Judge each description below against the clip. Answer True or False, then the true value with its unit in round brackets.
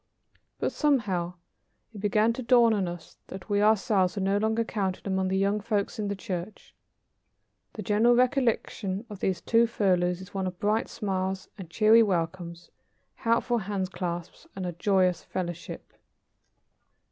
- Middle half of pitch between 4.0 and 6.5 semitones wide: False (3.0 semitones)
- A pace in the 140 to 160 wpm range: True (150 wpm)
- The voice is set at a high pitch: True (195 Hz)